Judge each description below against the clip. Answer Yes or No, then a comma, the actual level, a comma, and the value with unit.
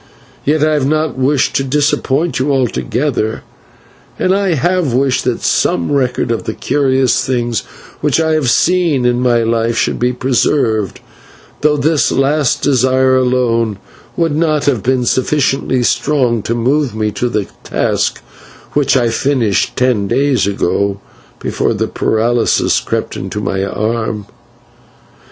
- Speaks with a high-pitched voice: No, low, 130 Hz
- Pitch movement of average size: Yes, average, 3.9 semitones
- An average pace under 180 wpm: Yes, average, 140 wpm